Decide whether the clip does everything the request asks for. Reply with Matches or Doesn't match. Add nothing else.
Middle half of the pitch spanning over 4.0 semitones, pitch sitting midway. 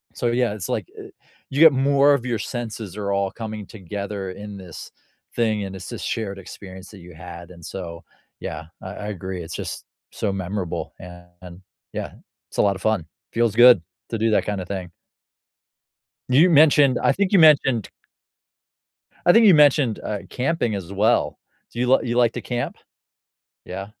Doesn't match